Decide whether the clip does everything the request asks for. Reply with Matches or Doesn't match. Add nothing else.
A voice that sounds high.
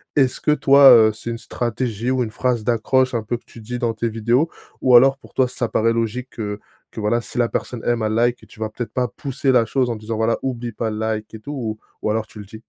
Doesn't match